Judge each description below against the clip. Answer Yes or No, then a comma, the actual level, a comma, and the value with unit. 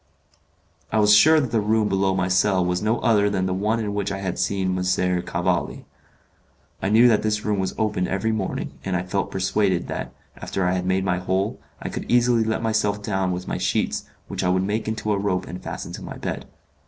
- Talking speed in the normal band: No, fast, 225 wpm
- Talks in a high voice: No, low, 100 Hz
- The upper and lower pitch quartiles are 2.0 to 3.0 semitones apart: Yes, narrow, 2.6 semitones